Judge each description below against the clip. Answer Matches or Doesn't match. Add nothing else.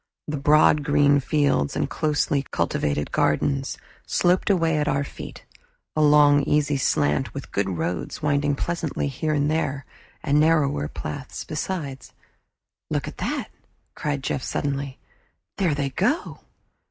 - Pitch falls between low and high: Matches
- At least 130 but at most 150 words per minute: Matches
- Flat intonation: Matches